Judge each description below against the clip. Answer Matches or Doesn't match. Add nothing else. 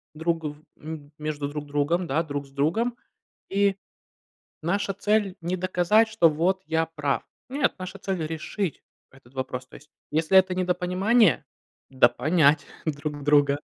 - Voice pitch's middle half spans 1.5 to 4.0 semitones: Doesn't match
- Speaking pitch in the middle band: Matches